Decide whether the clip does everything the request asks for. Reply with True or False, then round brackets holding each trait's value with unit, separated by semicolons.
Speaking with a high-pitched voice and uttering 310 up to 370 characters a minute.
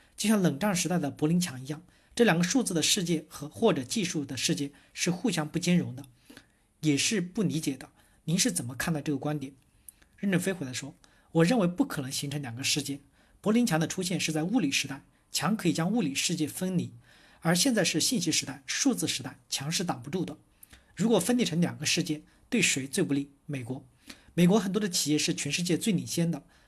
False (160 Hz; 315 characters per minute)